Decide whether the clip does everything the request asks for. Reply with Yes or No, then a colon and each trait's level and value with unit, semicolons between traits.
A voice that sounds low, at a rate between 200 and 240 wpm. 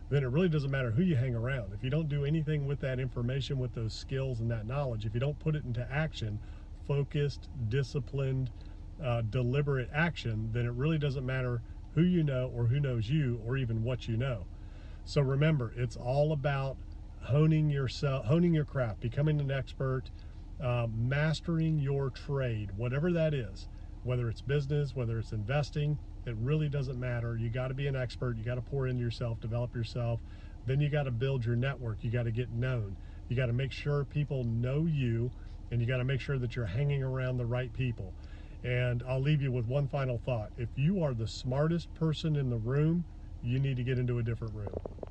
Yes: low, 125 Hz; fast, 205 wpm